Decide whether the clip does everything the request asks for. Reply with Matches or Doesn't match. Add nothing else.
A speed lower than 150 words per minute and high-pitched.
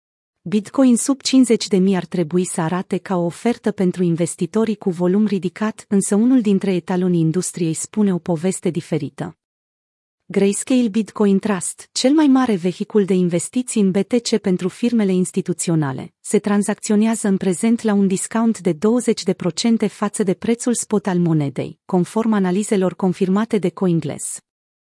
Matches